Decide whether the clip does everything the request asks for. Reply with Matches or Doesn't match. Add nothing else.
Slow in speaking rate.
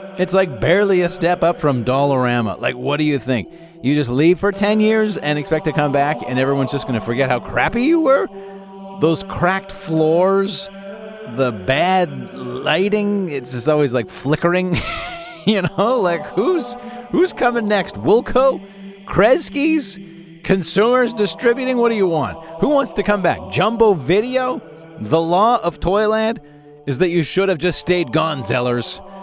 Doesn't match